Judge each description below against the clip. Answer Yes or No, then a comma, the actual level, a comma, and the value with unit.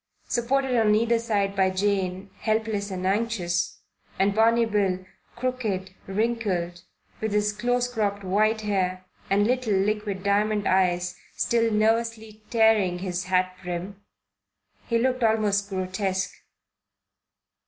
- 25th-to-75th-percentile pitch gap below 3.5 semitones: Yes, average, 3.0 semitones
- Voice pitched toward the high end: Yes, high, 205 Hz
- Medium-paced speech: No, slow, 120 wpm